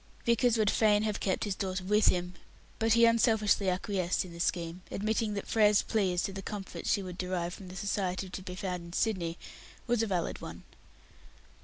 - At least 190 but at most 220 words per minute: Yes, average, 200 wpm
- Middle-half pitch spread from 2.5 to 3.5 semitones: Yes, average, 2.8 semitones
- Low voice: No, high, 195 Hz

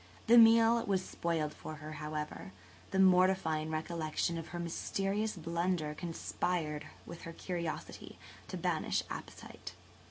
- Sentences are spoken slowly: Yes, slow, 125 wpm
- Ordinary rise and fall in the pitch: Yes, average, 3.2 semitones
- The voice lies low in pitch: No, medium, 170 Hz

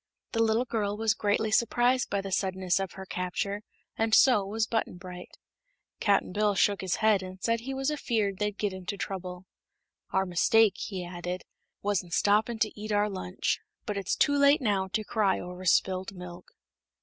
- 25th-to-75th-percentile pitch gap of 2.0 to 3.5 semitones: Yes, average, 2.9 semitones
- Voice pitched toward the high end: Yes, high, 200 Hz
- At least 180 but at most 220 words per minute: Yes, average, 185 wpm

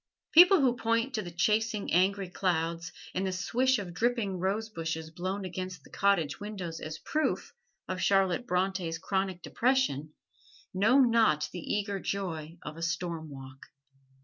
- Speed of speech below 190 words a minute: Yes, average, 150 wpm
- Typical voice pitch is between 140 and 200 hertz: Yes, high, 190 Hz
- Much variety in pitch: No, average, 4.5 semitones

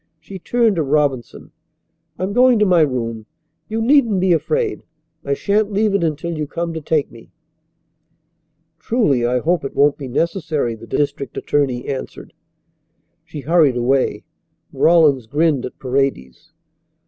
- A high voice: No, medium, 155 Hz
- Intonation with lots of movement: Yes, wide, 5.8 semitones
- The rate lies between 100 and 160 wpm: Yes, average, 150 wpm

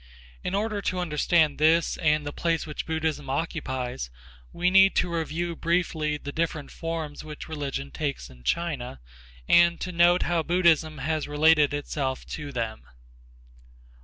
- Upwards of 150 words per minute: No, average, 145 wpm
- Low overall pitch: No, medium, 155 Hz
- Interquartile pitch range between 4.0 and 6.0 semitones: No, average, 2.8 semitones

